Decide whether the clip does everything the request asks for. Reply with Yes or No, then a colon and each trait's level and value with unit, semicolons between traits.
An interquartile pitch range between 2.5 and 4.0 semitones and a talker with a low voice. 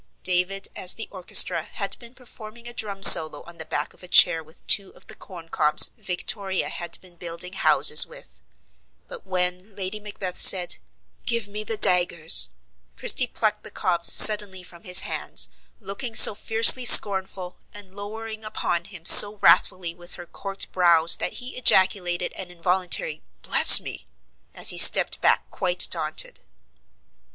No: average, 3.1 semitones; medium, 185 Hz